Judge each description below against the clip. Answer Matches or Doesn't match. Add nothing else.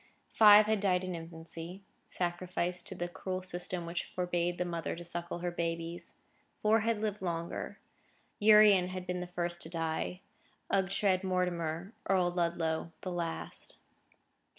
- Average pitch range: Doesn't match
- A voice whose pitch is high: Doesn't match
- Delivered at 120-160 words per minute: Matches